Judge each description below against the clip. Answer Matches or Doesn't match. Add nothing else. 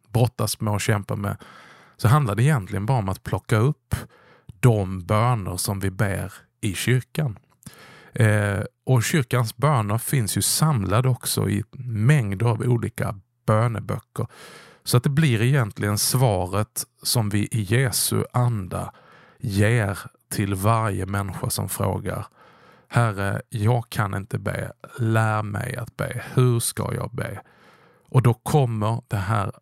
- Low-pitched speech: Matches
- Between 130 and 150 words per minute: Matches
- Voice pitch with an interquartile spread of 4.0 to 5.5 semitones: Doesn't match